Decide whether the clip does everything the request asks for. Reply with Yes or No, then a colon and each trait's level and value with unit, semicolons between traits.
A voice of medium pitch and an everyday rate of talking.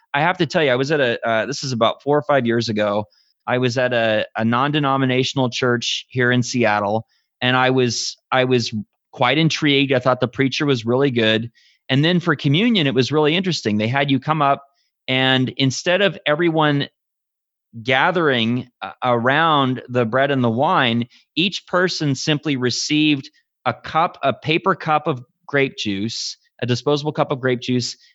No: low, 130 Hz; average, 180 wpm